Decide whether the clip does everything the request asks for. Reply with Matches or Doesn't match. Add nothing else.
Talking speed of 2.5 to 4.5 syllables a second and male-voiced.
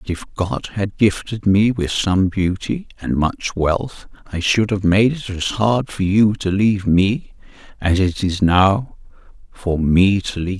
Matches